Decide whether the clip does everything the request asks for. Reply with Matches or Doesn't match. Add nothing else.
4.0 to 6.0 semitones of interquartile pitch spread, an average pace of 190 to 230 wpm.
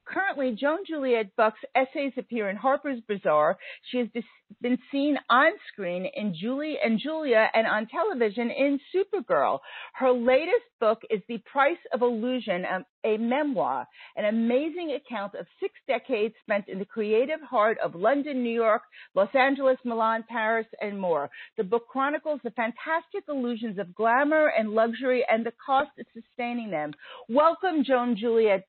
Doesn't match